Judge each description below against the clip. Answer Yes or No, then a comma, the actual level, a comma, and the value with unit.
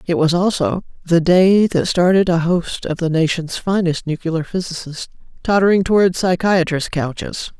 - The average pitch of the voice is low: No, medium, 170 Hz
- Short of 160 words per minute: Yes, average, 150 wpm